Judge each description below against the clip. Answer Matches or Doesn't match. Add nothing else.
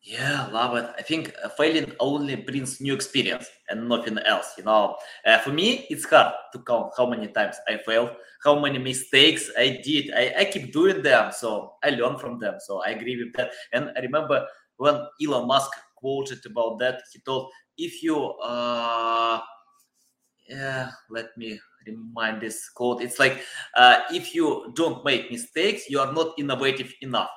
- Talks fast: Doesn't match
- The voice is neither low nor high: Doesn't match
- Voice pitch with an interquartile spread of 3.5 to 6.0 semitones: Matches